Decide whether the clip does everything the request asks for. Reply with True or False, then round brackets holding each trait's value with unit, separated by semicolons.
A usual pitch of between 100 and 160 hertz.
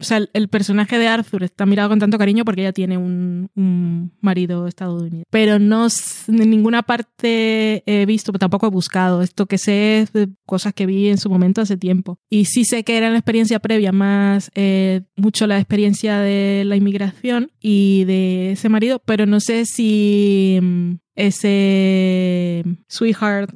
False (200 Hz)